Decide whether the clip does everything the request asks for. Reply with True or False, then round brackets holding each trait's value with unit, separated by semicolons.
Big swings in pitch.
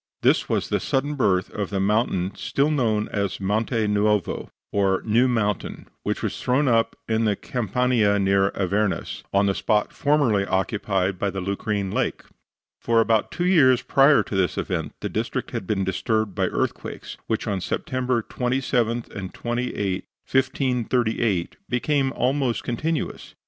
False (4.1 semitones)